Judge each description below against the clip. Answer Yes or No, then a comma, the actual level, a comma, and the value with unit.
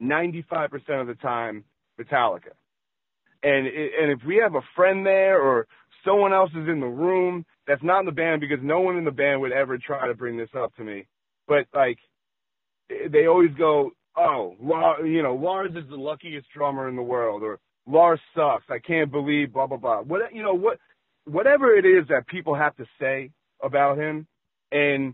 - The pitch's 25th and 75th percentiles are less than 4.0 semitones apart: No, average, 5.2 semitones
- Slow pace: No, average, 200 wpm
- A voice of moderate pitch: Yes, medium, 155 Hz